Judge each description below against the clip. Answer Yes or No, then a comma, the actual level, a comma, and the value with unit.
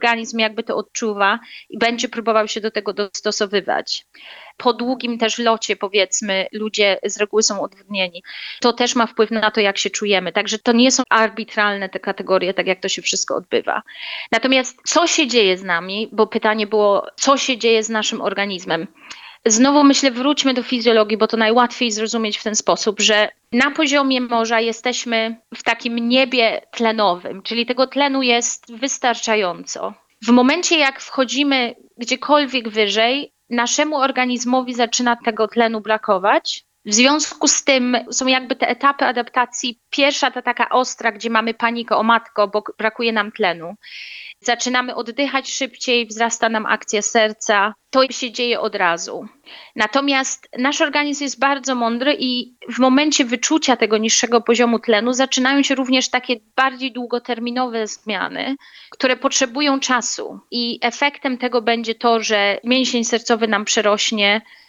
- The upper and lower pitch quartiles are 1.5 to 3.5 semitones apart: Yes, average, 3.1 semitones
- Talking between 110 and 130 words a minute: No, average, 150 wpm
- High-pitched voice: Yes, high, 235 Hz